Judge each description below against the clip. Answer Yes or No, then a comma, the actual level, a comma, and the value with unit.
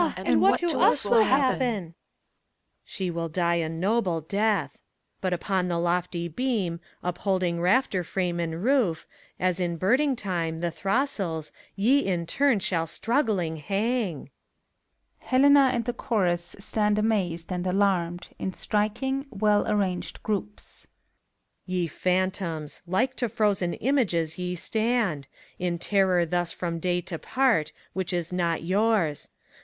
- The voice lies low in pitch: No, medium, 185 Hz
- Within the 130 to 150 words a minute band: Yes, average, 145 wpm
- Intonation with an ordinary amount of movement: Yes, average, 4.2 semitones